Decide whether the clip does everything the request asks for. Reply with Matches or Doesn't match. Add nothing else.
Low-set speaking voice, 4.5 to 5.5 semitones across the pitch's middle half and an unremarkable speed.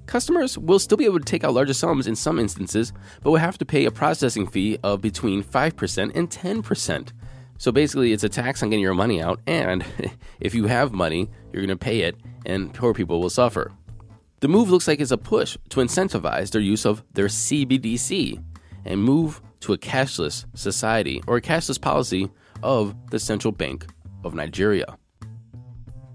Matches